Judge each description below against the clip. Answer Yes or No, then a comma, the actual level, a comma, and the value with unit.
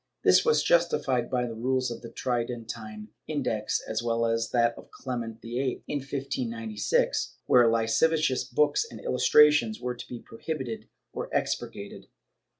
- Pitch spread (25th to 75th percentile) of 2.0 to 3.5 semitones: Yes, narrow, 2.5 semitones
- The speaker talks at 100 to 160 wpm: Yes, average, 150 wpm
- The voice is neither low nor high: No, low, 120 Hz